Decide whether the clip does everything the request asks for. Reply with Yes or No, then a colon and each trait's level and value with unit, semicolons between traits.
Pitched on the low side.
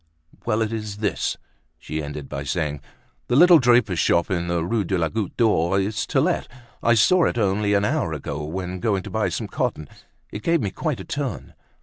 Yes: low, 100 Hz